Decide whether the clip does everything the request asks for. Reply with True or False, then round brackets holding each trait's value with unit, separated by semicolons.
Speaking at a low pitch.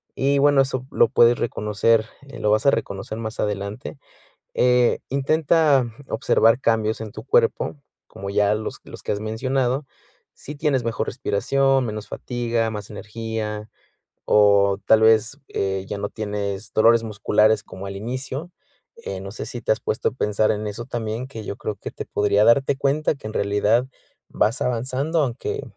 True (115 Hz)